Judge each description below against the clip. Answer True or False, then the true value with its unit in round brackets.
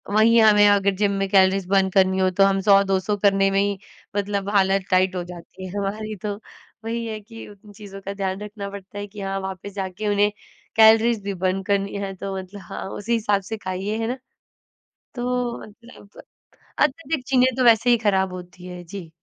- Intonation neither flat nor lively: False (1.9 semitones)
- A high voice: True (200 Hz)